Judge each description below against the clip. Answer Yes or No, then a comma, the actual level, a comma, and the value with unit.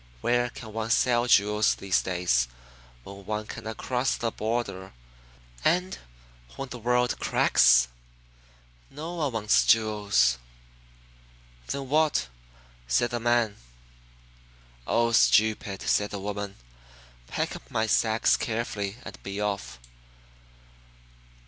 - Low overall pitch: Yes, low, 110 Hz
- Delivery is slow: Yes, slow, 110 wpm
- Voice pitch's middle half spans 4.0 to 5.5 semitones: No, average, 3.4 semitones